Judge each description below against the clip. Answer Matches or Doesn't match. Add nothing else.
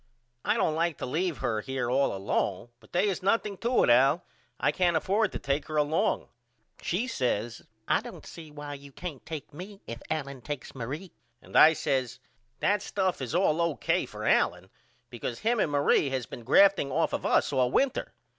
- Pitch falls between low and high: Matches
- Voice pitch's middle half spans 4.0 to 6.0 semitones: Matches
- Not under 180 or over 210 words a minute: Matches